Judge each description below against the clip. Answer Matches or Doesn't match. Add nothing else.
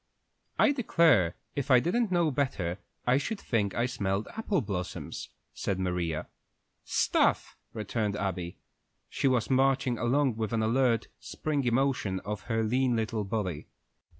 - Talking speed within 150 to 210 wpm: Doesn't match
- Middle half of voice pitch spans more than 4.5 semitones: Matches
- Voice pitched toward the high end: Doesn't match